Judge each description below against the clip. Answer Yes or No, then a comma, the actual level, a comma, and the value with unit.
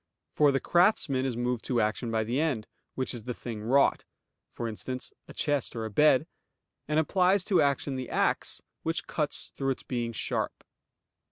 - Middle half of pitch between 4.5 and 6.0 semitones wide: No, average, 4.1 semitones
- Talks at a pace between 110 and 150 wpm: No, average, 180 wpm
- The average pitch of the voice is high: No, low, 130 Hz